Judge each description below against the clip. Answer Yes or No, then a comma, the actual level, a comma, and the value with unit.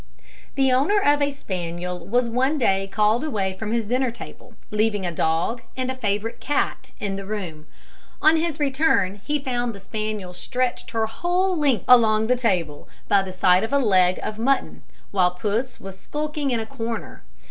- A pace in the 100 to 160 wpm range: No, average, 180 wpm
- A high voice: Yes, high, 225 Hz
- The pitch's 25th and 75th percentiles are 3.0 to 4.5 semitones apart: No, wide, 5.4 semitones